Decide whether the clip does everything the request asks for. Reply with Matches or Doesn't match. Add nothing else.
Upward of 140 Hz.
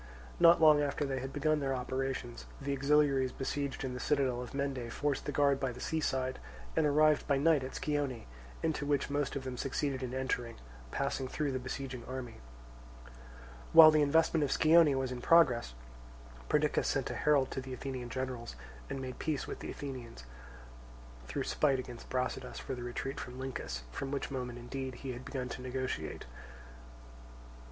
Doesn't match